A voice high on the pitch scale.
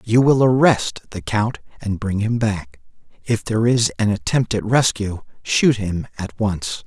No: low, 115 Hz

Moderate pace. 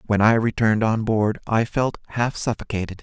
Yes: average, 180 wpm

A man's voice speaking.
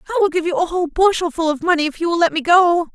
No: female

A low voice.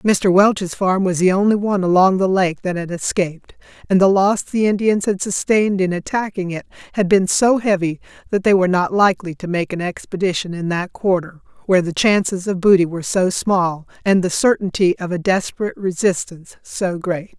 No: medium, 185 Hz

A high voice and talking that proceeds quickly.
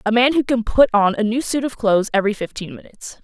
Yes: high, 225 Hz; fast, 260 wpm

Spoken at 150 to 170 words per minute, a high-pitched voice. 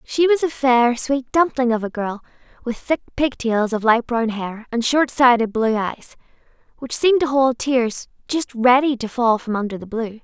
No: fast, 205 wpm; high, 245 Hz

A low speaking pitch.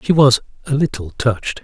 Yes: low, 130 Hz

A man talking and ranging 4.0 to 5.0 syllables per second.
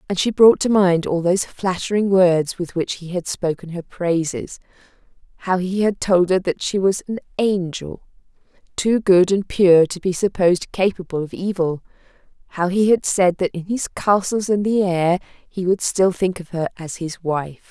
No: female; 4.6 syllables/s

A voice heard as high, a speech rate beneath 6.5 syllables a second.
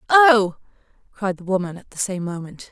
Yes: high, 200 Hz; 5.1 syllables/s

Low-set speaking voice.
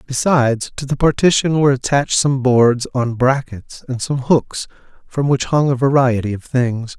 Yes: low, 130 Hz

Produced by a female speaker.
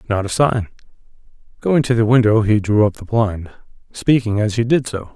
No: male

